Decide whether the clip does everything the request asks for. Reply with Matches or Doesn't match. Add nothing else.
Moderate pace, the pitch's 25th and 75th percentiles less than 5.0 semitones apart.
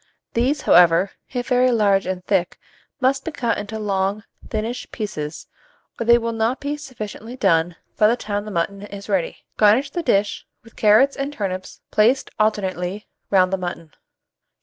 Matches